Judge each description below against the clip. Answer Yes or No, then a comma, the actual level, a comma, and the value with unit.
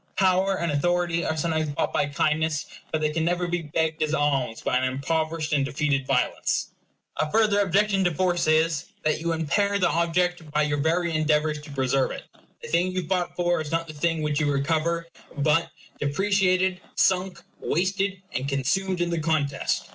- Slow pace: No, average, 185 wpm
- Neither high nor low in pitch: Yes, medium, 160 Hz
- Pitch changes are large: No, average, 3.0 semitones